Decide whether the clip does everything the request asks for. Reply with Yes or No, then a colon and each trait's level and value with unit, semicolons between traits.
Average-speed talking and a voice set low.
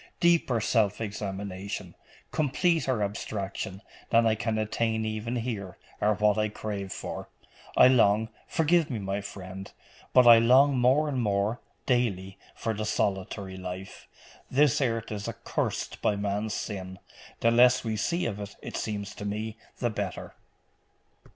Yes: average, 145 wpm; low, 110 Hz